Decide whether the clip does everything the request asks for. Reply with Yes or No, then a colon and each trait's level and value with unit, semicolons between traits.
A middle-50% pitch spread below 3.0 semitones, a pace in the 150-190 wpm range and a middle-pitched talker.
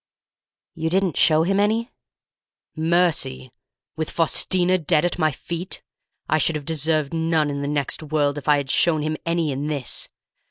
Yes: narrow, 2.6 semitones; average, 165 wpm; medium, 155 Hz